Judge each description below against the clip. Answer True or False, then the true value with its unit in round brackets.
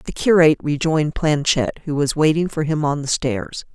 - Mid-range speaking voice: True (150 Hz)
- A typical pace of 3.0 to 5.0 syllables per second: False (5.3 syllables/s)